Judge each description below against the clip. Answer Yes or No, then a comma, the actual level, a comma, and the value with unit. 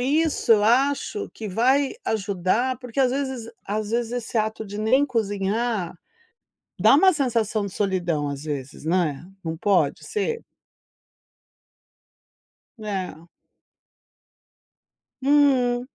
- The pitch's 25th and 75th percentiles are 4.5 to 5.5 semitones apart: Yes, average, 5.1 semitones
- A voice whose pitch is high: Yes, high, 220 Hz